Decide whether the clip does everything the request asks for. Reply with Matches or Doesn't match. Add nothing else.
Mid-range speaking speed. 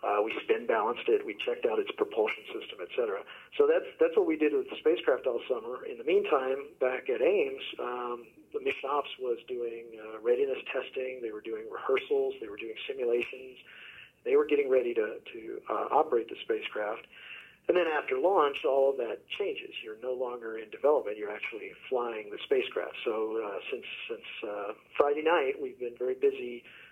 Matches